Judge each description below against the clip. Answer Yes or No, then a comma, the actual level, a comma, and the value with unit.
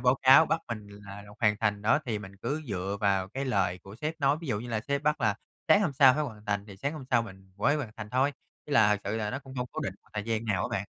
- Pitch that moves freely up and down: No, average, 5.0 semitones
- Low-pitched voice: Yes, low, 110 Hz